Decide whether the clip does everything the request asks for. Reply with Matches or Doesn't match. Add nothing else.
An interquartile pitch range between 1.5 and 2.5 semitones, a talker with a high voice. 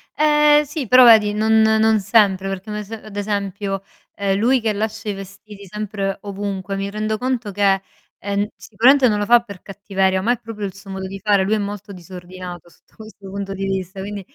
Matches